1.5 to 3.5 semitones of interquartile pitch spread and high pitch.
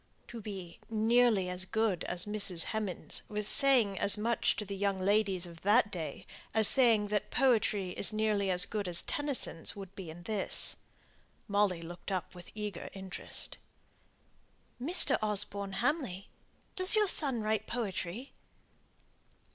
Yes: average, 2.9 semitones; high, 205 Hz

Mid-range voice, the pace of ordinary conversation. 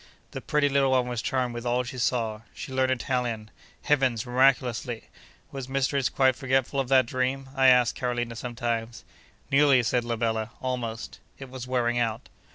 No: low, 125 Hz; average, 160 wpm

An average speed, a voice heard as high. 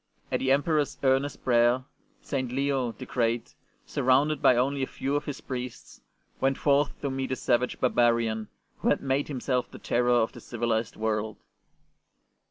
No: average, 165 wpm; low, 130 Hz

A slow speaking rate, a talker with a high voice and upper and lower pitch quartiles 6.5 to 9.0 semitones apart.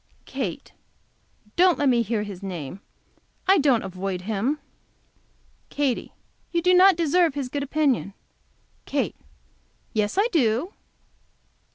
Yes: slow, 120 wpm; very high, 265 Hz; wide, 8.1 semitones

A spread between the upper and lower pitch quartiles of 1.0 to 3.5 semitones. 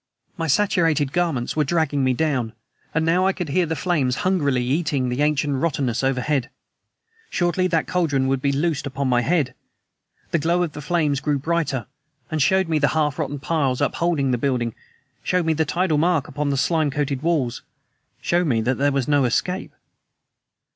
No: average, 3.9 semitones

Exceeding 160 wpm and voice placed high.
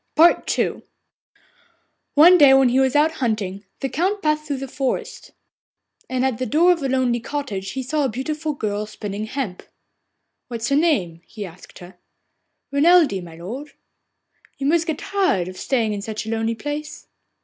Yes: average, 170 wpm; very high, 265 Hz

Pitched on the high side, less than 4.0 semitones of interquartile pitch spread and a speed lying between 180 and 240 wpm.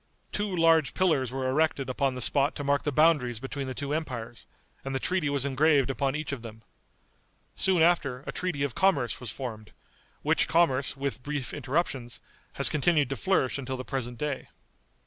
No: medium, 140 Hz; average, 3.1 semitones; average, 185 wpm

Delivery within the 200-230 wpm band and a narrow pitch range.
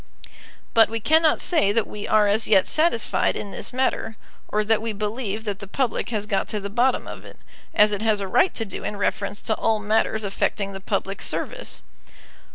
Yes: fast, 205 wpm; narrow, 2.1 semitones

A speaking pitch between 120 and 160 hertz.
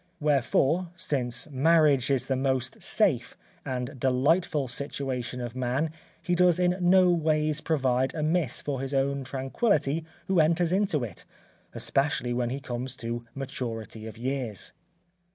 Yes: low, 135 Hz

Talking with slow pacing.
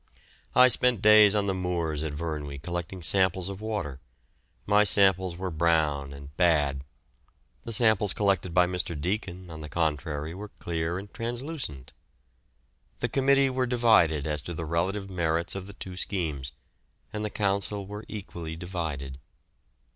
No: average, 150 wpm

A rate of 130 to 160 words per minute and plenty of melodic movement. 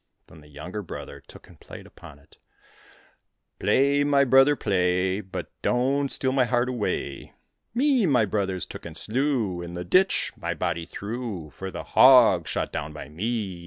No: average, 175 wpm; wide, 6.8 semitones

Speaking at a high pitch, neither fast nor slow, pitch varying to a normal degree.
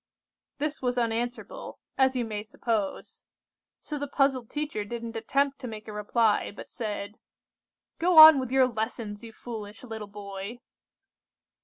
Yes: high, 230 Hz; average, 145 wpm; average, 3.8 semitones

